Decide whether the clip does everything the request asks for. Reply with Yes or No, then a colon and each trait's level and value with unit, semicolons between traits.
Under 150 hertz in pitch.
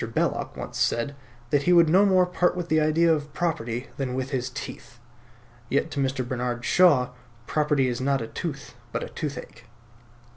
Yes: medium, 140 Hz